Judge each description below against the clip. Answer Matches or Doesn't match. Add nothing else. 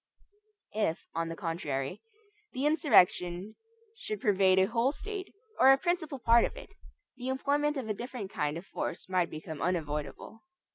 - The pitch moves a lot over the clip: Matches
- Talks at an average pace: Matches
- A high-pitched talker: Matches